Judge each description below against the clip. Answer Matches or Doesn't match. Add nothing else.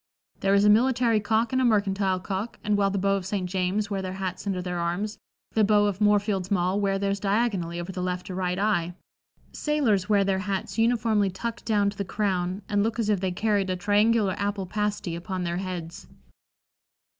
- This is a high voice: Matches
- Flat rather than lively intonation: Matches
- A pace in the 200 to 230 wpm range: Matches